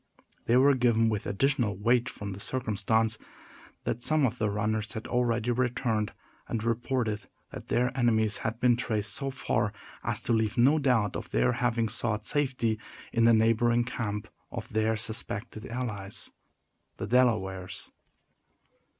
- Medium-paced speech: Yes, average, 150 wpm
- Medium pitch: No, low, 115 Hz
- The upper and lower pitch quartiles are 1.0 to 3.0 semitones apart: Yes, narrow, 2.4 semitones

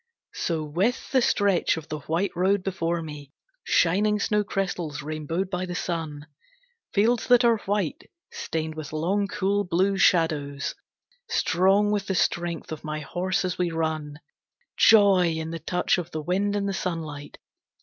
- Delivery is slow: No, average, 155 wpm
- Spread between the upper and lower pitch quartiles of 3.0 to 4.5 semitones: Yes, average, 4.0 semitones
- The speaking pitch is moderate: Yes, medium, 180 Hz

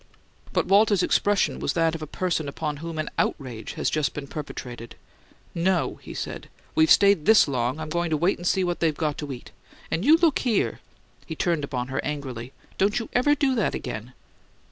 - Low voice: No, medium, 160 Hz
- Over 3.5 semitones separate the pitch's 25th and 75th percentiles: Yes, average, 5.3 semitones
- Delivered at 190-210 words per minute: Yes, average, 200 wpm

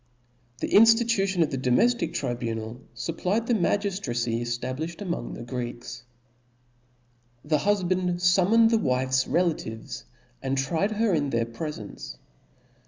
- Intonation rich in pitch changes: Yes, wide, 8.1 semitones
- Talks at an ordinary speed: No, slow, 130 wpm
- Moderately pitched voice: Yes, medium, 150 Hz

